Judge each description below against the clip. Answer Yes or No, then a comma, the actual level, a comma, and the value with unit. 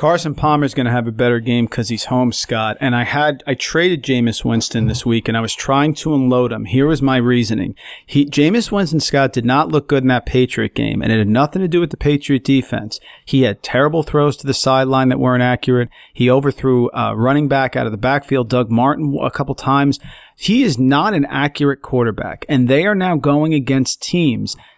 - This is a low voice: Yes, low, 130 Hz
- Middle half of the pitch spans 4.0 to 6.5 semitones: No, average, 3.1 semitones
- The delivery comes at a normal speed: No, fast, 225 wpm